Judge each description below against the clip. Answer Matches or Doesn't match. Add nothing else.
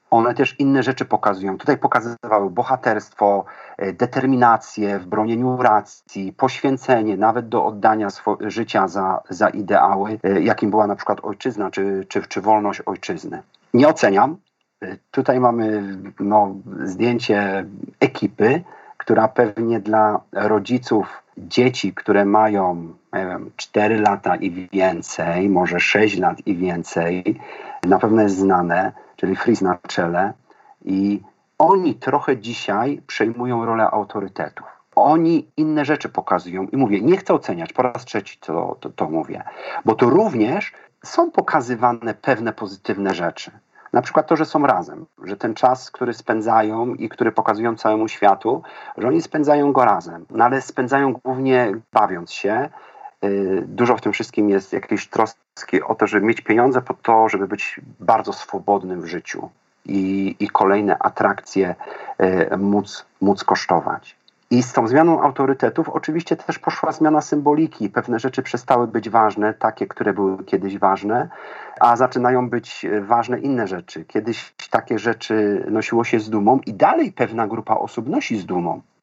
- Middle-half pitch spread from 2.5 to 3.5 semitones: Doesn't match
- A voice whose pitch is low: Matches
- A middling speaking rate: Matches